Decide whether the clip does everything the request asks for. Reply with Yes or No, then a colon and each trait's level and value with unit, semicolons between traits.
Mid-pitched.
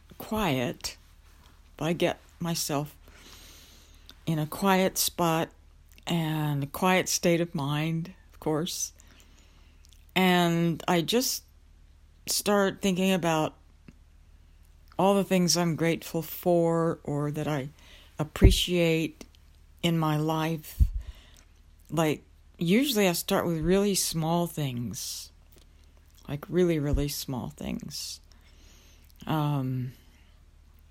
Yes: medium, 145 Hz